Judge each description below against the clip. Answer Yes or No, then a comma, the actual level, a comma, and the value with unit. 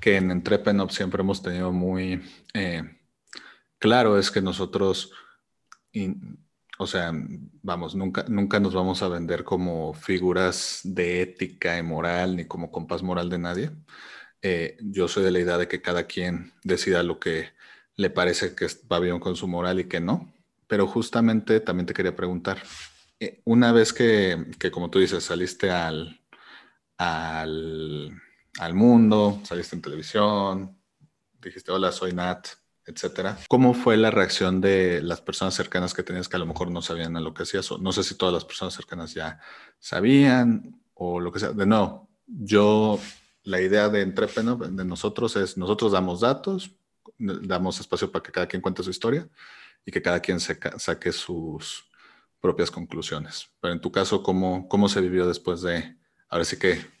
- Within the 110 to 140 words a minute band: No, average, 170 wpm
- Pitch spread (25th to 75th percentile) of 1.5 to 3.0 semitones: Yes, average, 2.7 semitones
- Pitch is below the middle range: Yes, very low, 95 Hz